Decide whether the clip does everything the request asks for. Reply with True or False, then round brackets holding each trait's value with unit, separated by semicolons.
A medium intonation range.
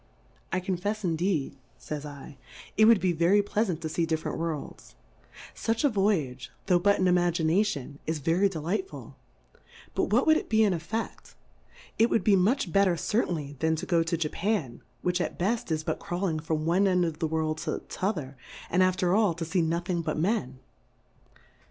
True (3.9 semitones)